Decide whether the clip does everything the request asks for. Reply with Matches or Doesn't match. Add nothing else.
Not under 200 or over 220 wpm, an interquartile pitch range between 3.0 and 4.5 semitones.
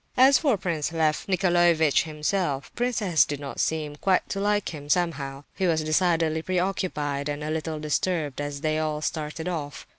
Doesn't match